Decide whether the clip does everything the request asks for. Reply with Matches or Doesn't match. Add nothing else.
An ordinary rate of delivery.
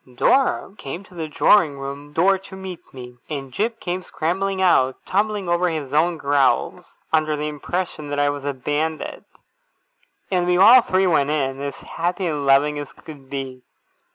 Matches